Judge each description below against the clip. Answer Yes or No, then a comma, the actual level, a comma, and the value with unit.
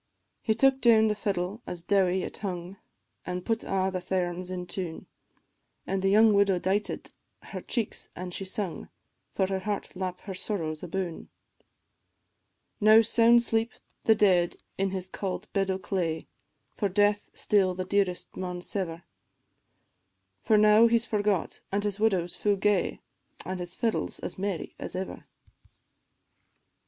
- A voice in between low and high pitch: No, high, 195 Hz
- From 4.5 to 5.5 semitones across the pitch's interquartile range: No, narrow, 2.6 semitones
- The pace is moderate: Yes, average, 150 wpm